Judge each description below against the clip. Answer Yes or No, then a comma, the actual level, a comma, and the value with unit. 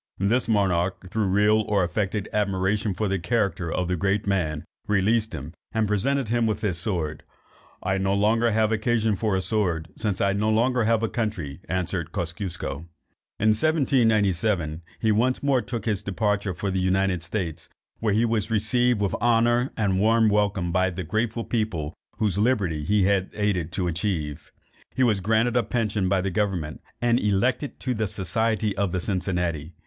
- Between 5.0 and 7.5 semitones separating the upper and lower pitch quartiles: No, average, 3.3 semitones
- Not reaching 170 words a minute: No, average, 175 wpm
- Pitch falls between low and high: No, low, 105 Hz